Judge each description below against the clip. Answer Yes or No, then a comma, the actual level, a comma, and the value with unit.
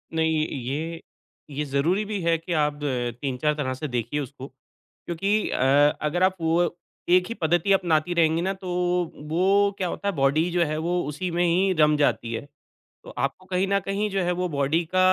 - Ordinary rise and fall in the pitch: Yes, average, 3.9 semitones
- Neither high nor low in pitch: Yes, medium, 165 Hz